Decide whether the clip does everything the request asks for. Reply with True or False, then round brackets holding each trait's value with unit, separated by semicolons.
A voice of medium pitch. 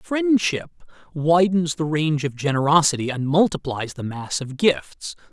True (155 Hz)